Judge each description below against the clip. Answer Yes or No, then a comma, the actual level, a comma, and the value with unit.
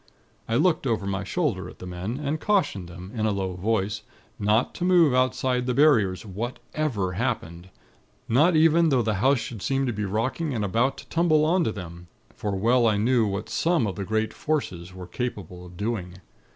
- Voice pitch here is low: Yes, low, 115 Hz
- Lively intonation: Yes, wide, 5.8 semitones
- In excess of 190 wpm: Yes, average, 200 wpm